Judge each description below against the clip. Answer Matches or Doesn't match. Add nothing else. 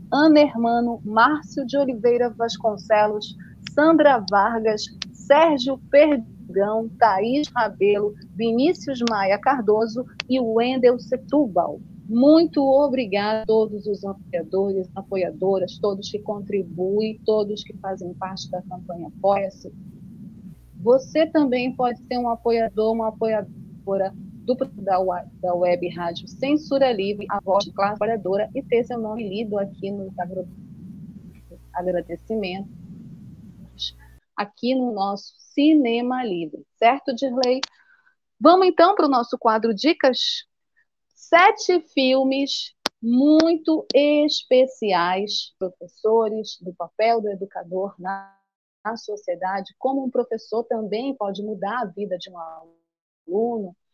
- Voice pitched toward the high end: Matches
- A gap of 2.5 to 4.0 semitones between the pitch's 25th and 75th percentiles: Doesn't match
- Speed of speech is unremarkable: Doesn't match